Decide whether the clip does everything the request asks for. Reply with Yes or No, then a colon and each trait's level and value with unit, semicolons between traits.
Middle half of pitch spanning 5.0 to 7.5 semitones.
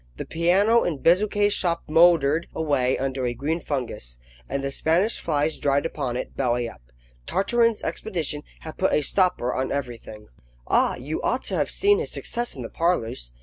Yes: wide, 5.6 semitones